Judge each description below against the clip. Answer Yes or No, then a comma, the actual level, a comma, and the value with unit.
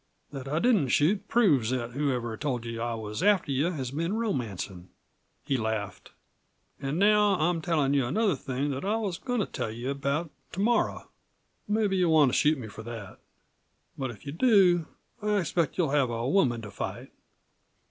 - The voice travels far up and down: Yes, wide, 7.3 semitones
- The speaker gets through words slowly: No, average, 185 wpm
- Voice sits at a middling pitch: Yes, medium, 145 Hz